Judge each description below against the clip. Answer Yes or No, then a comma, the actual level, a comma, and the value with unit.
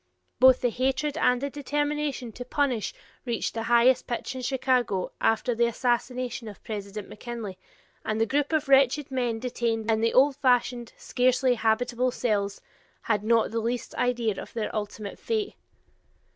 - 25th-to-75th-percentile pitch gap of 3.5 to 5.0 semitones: No, narrow, 2.6 semitones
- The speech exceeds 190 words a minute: No, average, 160 wpm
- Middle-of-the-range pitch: No, high, 245 Hz